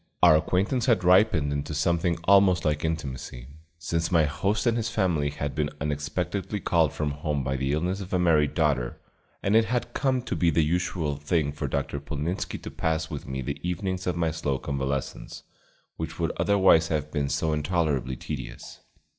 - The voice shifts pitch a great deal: No, average, 3.9 semitones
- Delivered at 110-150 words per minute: No, average, 180 wpm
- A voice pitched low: Yes, very low, 80 Hz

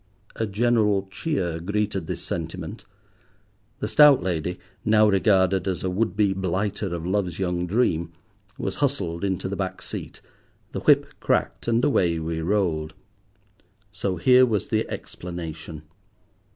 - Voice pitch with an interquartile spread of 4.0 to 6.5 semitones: No, average, 3.6 semitones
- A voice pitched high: No, very low, 95 Hz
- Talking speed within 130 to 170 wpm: Yes, average, 140 wpm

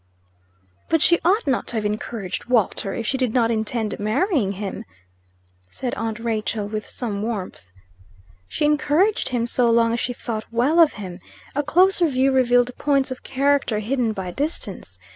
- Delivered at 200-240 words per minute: No, average, 165 wpm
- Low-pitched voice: No, high, 240 Hz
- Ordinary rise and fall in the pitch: Yes, average, 4.4 semitones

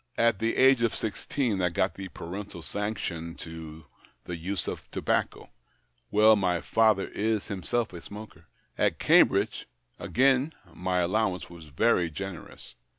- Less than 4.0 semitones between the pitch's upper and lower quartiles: No, average, 4.4 semitones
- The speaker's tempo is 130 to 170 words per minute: Yes, average, 150 wpm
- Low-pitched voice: Yes, very low, 95 Hz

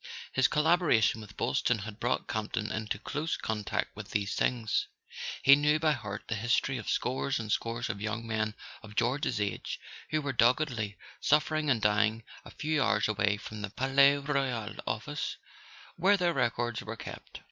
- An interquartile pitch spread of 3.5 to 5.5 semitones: Yes, average, 4.8 semitones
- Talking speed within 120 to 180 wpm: Yes, average, 170 wpm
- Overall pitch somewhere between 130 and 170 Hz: No, low, 120 Hz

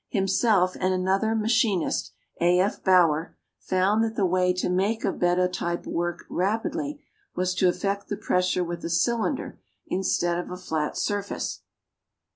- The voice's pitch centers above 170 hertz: Yes, medium, 185 Hz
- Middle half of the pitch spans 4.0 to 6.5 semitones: No, average, 2.7 semitones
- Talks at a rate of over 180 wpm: No, average, 155 wpm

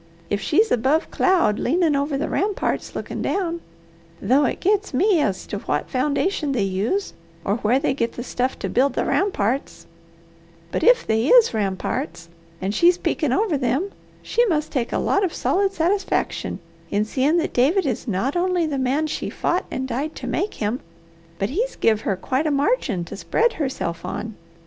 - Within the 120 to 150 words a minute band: No, average, 180 wpm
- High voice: Yes, very high, 280 Hz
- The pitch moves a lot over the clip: Yes, wide, 7.5 semitones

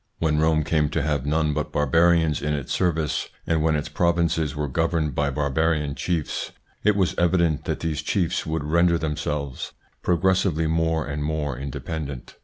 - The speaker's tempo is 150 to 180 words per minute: Yes, average, 165 wpm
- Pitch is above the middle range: No, very low, 80 Hz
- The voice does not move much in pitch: Yes, narrow, 1.9 semitones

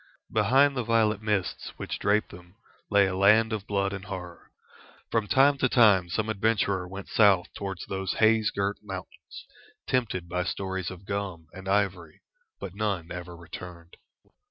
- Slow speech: No, average, 155 wpm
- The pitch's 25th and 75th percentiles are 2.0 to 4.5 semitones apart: Yes, average, 2.9 semitones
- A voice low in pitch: Yes, low, 100 Hz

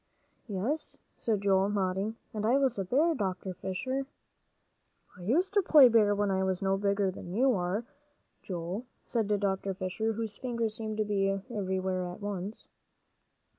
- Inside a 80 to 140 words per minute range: No, average, 160 wpm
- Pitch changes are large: No, average, 3.2 semitones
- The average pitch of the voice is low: No, high, 205 Hz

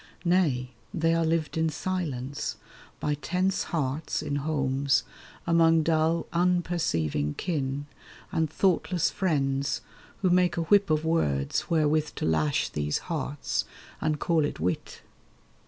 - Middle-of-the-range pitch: Yes, medium, 155 Hz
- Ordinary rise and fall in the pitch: Yes, average, 3.6 semitones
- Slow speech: Yes, slow, 125 wpm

